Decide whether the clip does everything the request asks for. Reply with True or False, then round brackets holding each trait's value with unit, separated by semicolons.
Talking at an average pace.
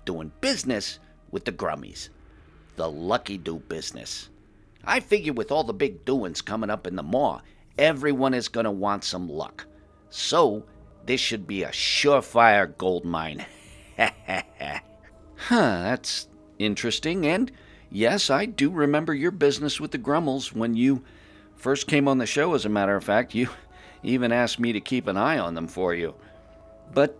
True (160 wpm)